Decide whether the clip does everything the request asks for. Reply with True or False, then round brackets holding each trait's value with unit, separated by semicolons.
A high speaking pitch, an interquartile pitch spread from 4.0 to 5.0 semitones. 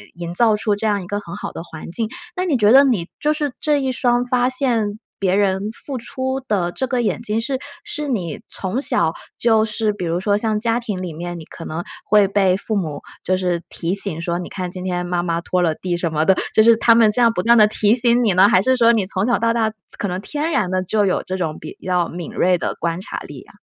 True (205 Hz; 4.7 semitones)